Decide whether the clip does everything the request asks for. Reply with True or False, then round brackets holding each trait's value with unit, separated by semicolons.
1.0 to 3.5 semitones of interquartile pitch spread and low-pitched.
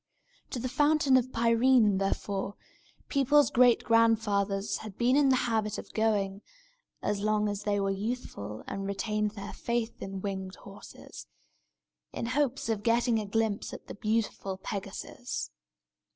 False (3.1 semitones; 215 Hz)